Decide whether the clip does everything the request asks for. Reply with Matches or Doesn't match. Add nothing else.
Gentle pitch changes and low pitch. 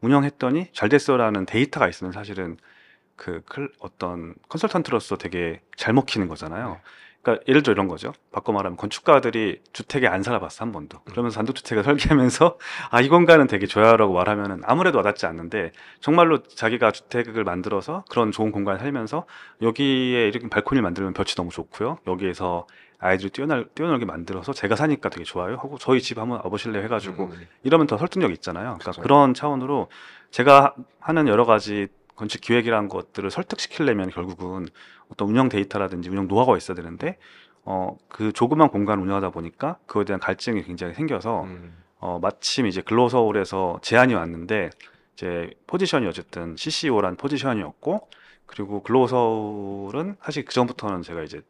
Doesn't match